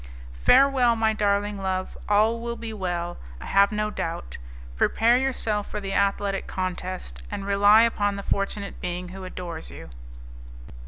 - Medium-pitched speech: No, high, 200 Hz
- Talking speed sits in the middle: Yes, average, 150 wpm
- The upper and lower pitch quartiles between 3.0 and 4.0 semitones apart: No, narrow, 2.6 semitones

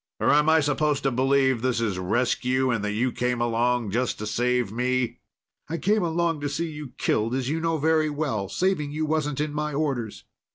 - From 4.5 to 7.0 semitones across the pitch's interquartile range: No, average, 4.0 semitones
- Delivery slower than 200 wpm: No, fast, 205 wpm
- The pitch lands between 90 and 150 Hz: Yes, low, 135 Hz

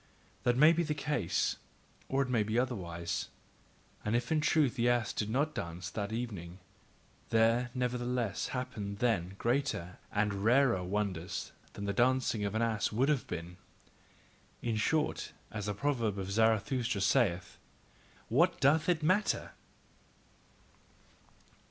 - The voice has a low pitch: Yes, low, 115 Hz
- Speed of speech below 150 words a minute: Yes, average, 140 wpm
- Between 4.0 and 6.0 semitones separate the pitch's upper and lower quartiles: Yes, average, 4.5 semitones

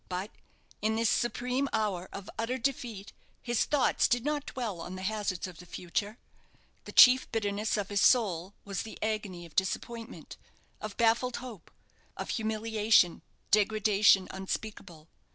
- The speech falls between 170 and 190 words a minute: No, average, 145 wpm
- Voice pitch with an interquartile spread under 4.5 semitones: Yes, average, 3.2 semitones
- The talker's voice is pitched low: No, high, 215 Hz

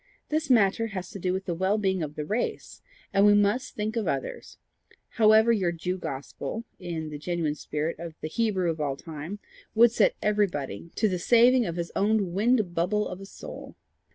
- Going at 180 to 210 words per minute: Yes, average, 195 wpm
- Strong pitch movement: No, average, 4.4 semitones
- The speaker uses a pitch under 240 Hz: Yes, high, 190 Hz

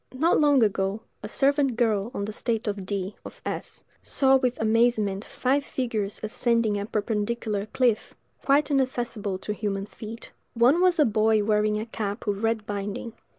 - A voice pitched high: Yes, high, 220 Hz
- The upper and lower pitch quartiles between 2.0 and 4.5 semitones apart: Yes, average, 3.2 semitones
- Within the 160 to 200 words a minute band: Yes, average, 165 wpm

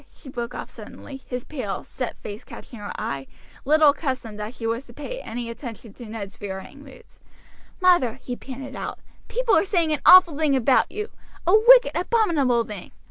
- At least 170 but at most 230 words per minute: Yes, average, 185 wpm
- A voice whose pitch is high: Yes, very high, 260 Hz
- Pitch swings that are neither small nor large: No, wide, 5.7 semitones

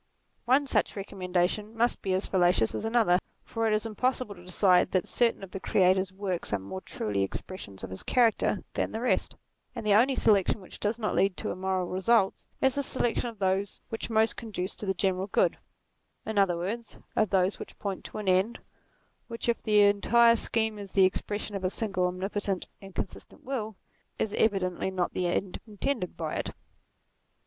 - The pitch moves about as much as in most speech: Yes, average, 3.2 semitones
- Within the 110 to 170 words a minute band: No, average, 190 wpm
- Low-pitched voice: No, high, 200 Hz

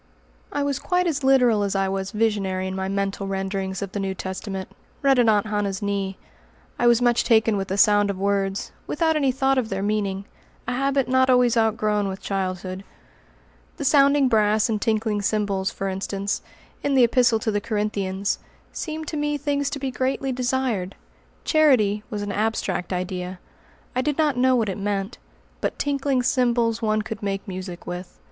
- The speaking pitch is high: Yes, high, 215 Hz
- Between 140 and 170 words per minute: No, average, 180 wpm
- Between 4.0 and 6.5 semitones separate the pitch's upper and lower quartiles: Yes, average, 4.8 semitones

